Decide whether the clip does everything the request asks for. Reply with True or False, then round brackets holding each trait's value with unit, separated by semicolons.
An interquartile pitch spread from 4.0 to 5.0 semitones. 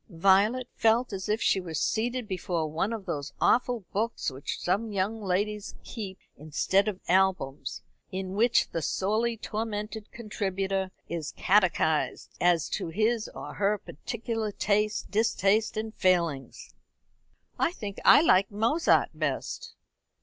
False (3.2 semitones)